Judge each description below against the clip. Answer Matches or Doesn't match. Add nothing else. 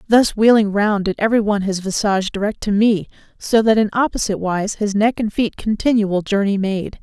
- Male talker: Doesn't match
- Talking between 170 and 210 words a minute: Matches